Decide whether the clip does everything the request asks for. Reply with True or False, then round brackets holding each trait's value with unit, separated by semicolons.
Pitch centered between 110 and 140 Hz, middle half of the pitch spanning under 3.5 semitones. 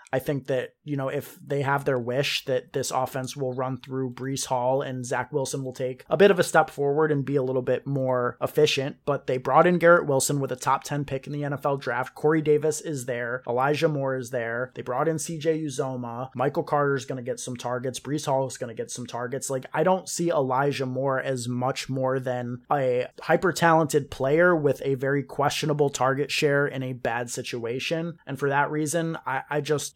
True (135 Hz; 2.6 semitones)